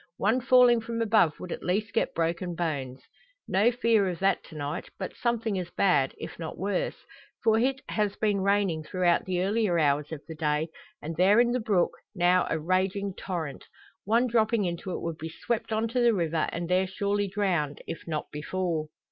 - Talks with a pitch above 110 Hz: Yes, medium, 185 Hz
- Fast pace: No, average, 195 wpm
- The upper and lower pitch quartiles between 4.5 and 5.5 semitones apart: Yes, average, 4.8 semitones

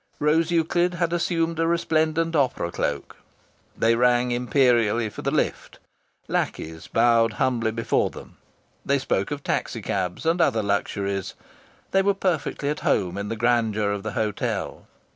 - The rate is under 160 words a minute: Yes, average, 150 wpm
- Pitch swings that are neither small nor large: No, wide, 7.1 semitones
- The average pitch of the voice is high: No, low, 125 Hz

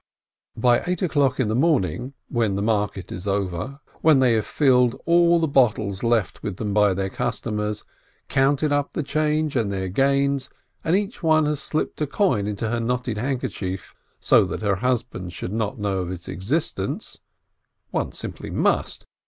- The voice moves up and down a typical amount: No, wide, 5.9 semitones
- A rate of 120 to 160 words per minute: No, average, 170 wpm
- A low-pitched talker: Yes, low, 120 Hz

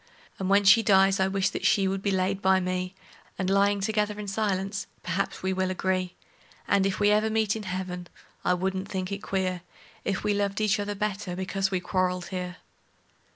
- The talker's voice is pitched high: Yes, high, 195 Hz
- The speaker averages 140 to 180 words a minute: No, average, 200 wpm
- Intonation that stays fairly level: Yes, narrow, 1.4 semitones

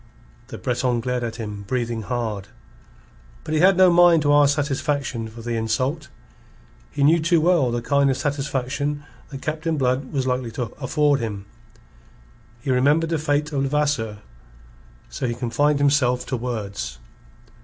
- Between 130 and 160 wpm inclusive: Yes, average, 155 wpm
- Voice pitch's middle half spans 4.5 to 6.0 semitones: No, average, 3.8 semitones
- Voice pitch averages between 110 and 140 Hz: Yes, low, 135 Hz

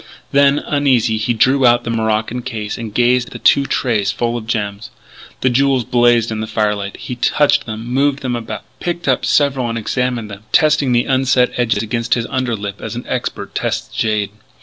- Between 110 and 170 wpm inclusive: No, average, 195 wpm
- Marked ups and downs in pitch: No, average, 2.9 semitones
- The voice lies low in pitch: Yes, low, 120 Hz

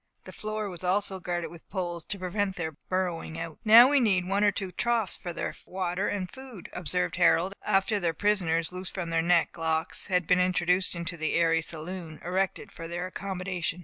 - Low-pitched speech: No, medium, 180 Hz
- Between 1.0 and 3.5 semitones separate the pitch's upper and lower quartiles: Yes, narrow, 2.4 semitones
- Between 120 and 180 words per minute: No, average, 195 wpm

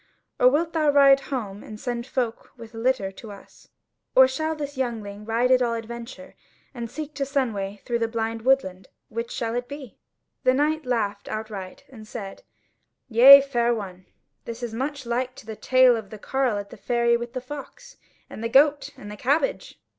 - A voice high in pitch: Yes, high, 240 Hz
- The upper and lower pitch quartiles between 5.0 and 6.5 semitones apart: No, average, 3.4 semitones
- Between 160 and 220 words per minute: Yes, average, 190 wpm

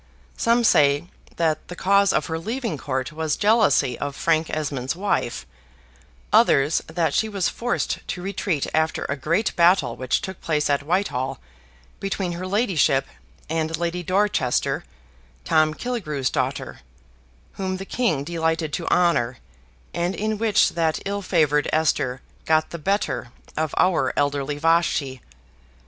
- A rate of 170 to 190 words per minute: No, average, 140 wpm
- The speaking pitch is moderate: Yes, medium, 165 Hz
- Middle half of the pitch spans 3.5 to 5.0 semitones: Yes, average, 4.7 semitones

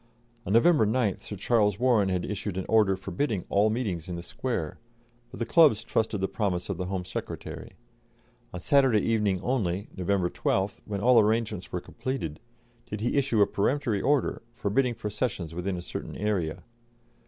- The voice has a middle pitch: No, low, 105 Hz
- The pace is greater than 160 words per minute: Yes, average, 170 wpm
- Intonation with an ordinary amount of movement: Yes, average, 3.9 semitones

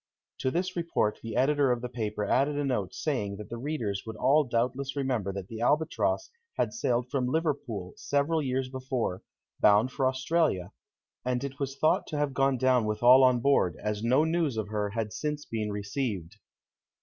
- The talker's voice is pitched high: No, low, 125 Hz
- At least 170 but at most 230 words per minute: Yes, average, 185 wpm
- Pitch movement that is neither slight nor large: Yes, average, 4.7 semitones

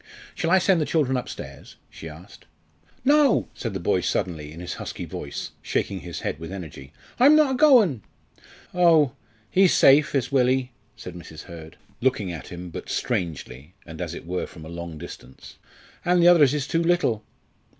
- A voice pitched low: Yes, low, 110 Hz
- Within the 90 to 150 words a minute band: No, average, 180 wpm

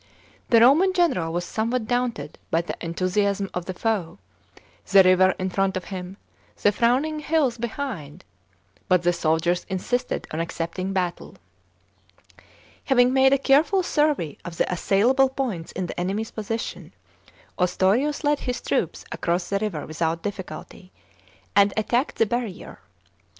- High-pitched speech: Yes, high, 200 Hz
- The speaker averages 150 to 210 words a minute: No, average, 140 wpm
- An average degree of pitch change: No, wide, 5.9 semitones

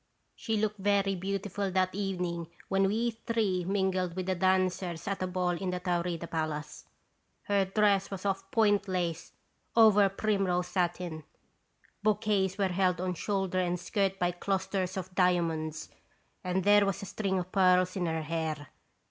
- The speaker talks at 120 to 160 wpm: Yes, average, 155 wpm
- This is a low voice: No, medium, 185 Hz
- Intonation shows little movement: Yes, narrow, 2.0 semitones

